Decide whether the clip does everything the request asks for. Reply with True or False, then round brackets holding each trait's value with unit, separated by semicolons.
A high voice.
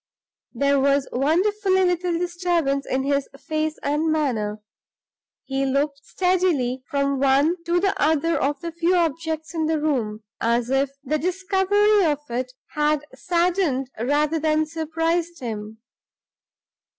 True (305 Hz)